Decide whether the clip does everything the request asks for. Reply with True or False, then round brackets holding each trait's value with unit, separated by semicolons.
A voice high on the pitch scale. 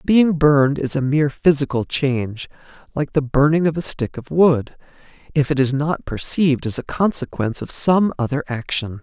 False (145 Hz)